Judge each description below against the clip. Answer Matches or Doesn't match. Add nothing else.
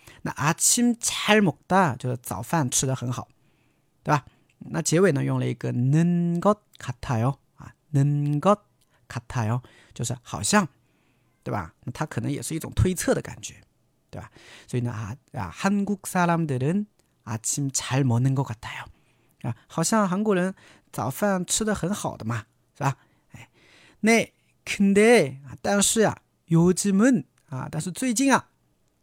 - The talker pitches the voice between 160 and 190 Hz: Doesn't match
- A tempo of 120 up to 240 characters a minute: Matches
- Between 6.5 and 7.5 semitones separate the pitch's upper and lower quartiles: Matches